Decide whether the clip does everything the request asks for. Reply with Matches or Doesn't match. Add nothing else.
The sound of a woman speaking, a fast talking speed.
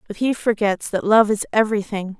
Doesn't match